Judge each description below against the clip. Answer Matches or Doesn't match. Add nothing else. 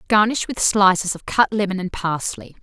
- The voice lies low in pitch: Doesn't match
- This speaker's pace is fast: Doesn't match